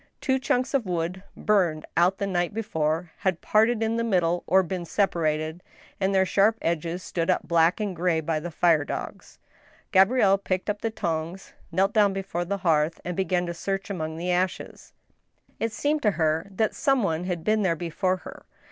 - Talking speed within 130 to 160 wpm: No, average, 190 wpm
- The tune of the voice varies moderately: Yes, average, 3.2 semitones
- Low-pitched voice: No, medium, 185 Hz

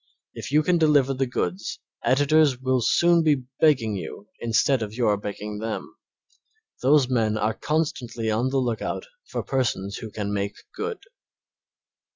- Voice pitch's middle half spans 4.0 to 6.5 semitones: Yes, average, 5.0 semitones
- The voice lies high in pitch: No, low, 125 Hz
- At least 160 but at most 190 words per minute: No, average, 150 wpm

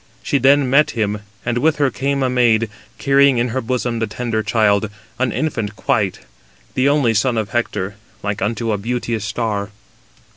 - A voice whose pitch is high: No, low, 115 Hz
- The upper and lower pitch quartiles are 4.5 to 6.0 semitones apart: No, average, 3.6 semitones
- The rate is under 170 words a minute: No, average, 175 wpm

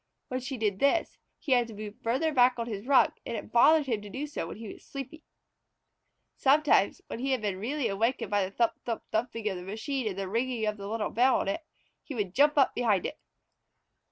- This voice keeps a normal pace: No, fast, 230 wpm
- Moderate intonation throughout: Yes, average, 4.3 semitones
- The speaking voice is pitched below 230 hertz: No, high, 235 Hz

